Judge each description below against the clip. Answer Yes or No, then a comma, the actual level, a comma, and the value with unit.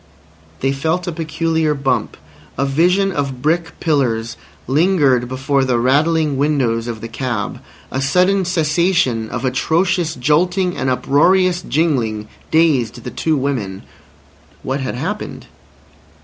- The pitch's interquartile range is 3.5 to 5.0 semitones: Yes, average, 4.7 semitones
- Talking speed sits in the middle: No, slow, 125 wpm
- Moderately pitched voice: Yes, medium, 145 Hz